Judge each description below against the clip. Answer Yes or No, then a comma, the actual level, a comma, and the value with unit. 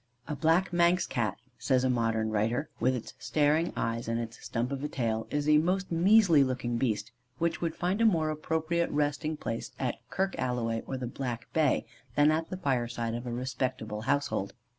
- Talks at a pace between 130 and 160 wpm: No, average, 190 wpm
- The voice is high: No, low, 135 Hz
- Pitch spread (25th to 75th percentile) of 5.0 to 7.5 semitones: Yes, wide, 5.4 semitones